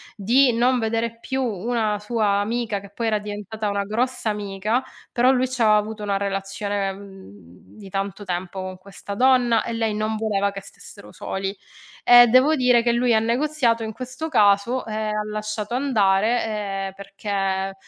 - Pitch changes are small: No, average, 3.1 semitones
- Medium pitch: No, high, 215 Hz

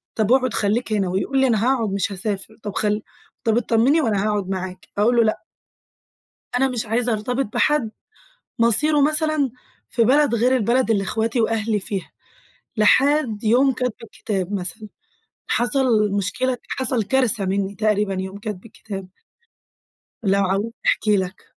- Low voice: No, high, 220 Hz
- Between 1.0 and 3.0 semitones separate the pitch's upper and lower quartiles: No, average, 3.7 semitones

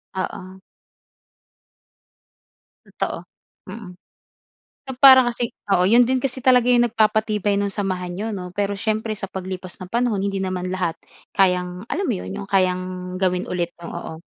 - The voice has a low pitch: No, high, 195 Hz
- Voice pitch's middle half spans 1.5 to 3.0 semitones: No, average, 3.7 semitones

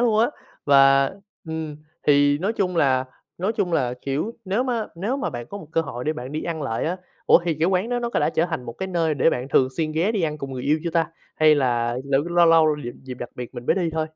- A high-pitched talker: No, medium, 155 Hz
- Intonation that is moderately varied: Yes, average, 4.5 semitones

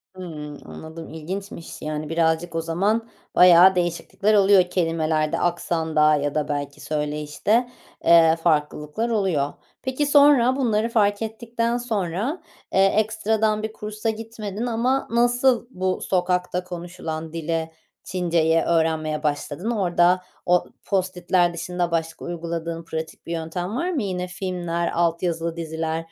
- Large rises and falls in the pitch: No, average, 4.7 semitones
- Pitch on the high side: No, medium, 175 Hz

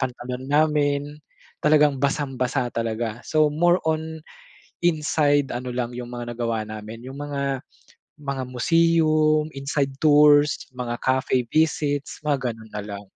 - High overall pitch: No, medium, 140 Hz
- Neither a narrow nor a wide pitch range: Yes, average, 3.5 semitones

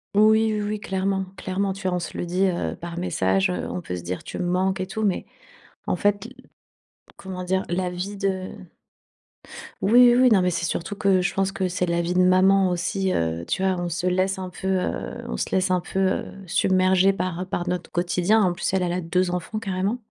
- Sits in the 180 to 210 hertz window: Yes, medium, 185 Hz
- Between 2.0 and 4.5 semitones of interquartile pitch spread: No, narrow, 1.6 semitones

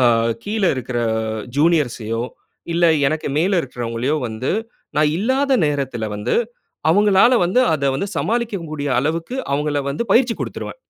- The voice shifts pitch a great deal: Yes, wide, 7.8 semitones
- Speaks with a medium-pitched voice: Yes, medium, 155 Hz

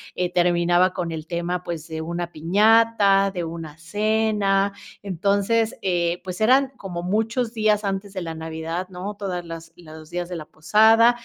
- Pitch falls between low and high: Yes, medium, 180 Hz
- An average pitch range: Yes, average, 3.6 semitones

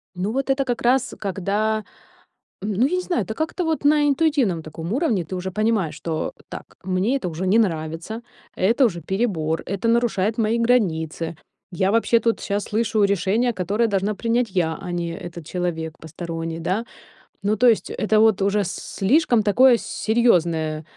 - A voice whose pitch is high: Yes, high, 205 Hz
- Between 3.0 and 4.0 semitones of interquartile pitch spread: No, average, 5.1 semitones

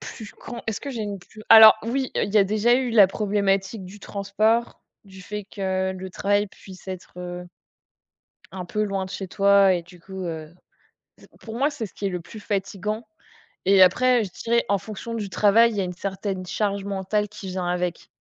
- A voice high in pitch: Yes, high, 200 Hz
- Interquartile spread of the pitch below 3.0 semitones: Yes, narrow, 2.4 semitones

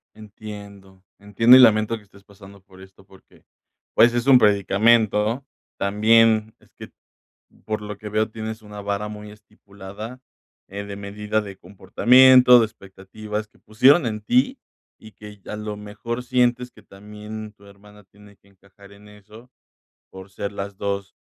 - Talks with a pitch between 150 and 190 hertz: No, low, 105 Hz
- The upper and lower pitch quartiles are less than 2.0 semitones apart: Yes, narrow, 1.6 semitones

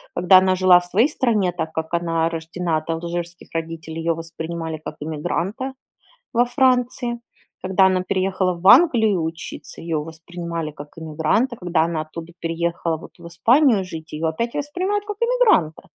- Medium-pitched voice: Yes, medium, 175 Hz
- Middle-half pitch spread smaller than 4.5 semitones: No, average, 4.9 semitones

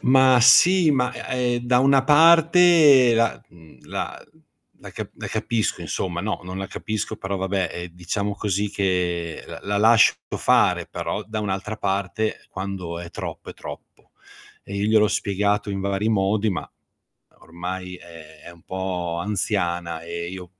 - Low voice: Yes, low, 100 Hz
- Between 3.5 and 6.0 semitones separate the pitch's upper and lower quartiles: Yes, average, 4.1 semitones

